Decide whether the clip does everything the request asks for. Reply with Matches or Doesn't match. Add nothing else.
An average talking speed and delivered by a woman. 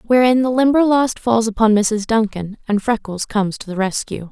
Matches